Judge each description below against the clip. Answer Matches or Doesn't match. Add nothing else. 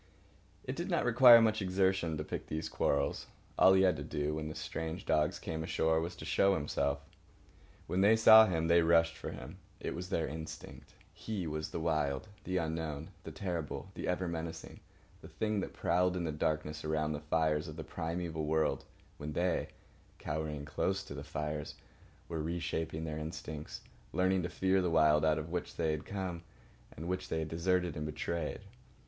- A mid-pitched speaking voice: Doesn't match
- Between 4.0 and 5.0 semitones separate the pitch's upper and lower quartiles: Doesn't match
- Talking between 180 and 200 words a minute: Matches